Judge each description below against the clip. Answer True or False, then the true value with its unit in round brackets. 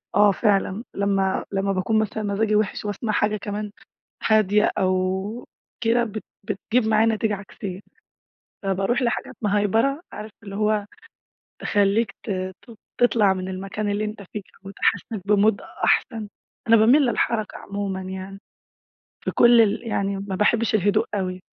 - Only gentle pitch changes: True (1.9 semitones)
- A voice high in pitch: True (210 Hz)